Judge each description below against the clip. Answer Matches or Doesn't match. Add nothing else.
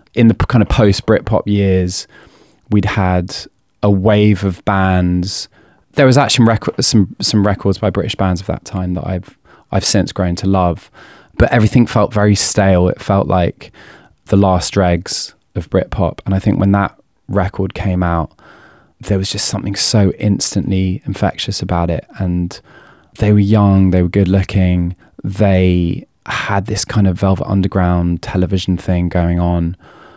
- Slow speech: Doesn't match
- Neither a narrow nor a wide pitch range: Doesn't match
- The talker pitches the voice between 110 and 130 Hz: Doesn't match